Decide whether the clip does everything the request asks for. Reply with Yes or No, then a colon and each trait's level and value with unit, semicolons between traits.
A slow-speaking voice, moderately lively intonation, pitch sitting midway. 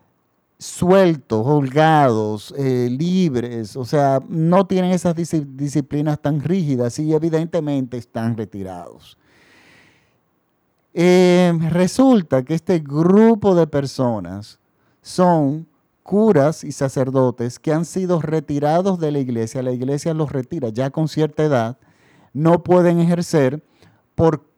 Yes: slow, 110 wpm; average, 4.6 semitones; medium, 150 Hz